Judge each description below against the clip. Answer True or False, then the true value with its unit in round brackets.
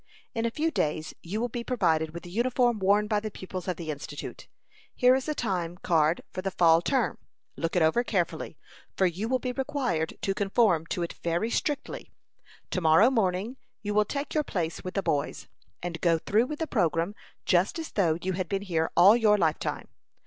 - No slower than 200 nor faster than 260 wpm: True (205 wpm)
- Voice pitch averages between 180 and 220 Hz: True (190 Hz)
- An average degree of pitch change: False (5.8 semitones)